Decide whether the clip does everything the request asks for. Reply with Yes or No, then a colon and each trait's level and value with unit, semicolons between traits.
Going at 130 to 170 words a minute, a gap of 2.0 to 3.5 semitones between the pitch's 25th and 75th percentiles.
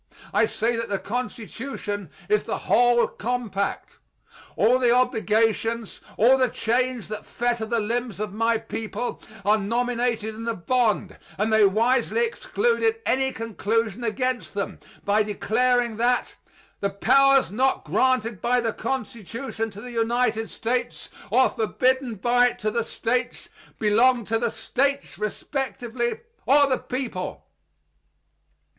Yes: slow, 135 wpm; narrow, 2.5 semitones